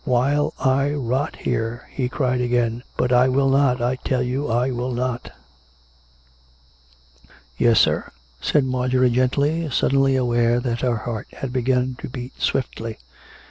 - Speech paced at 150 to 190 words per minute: Yes, average, 160 wpm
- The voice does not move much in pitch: Yes, narrow, 1.7 semitones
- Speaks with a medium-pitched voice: No, low, 125 Hz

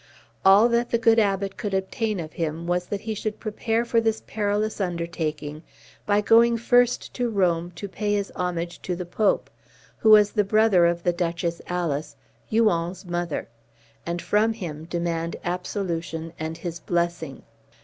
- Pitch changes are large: No, average, 4.1 semitones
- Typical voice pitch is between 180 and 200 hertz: Yes, medium, 185 Hz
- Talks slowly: No, average, 160 wpm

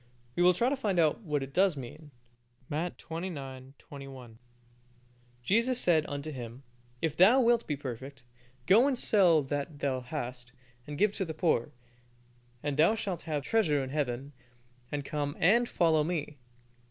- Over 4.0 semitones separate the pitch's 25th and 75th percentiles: Yes, average, 4.8 semitones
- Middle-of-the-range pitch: Yes, medium, 150 Hz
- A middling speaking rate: Yes, average, 160 wpm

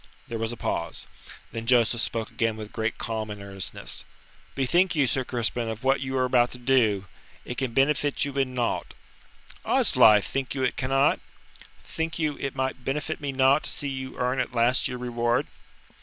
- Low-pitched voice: Yes, low, 125 Hz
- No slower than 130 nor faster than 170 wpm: No, average, 185 wpm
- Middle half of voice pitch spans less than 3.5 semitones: Yes, average, 2.8 semitones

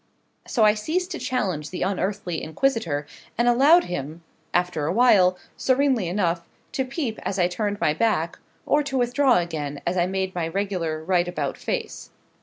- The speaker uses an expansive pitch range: Yes, wide, 6.2 semitones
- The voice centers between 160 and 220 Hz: Yes, high, 190 Hz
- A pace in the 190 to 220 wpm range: No, average, 170 wpm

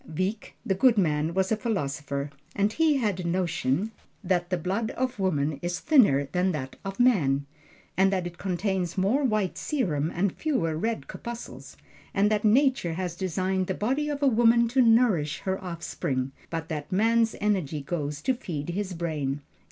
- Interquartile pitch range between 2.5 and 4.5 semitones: No, wide, 5.5 semitones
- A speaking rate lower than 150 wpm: No, average, 170 wpm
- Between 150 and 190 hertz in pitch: Yes, medium, 185 Hz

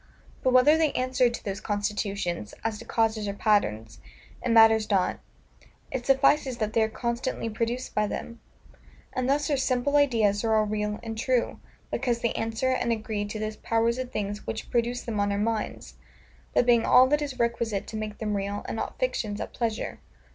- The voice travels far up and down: No, average, 2.9 semitones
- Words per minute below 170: No, average, 190 wpm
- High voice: Yes, high, 225 Hz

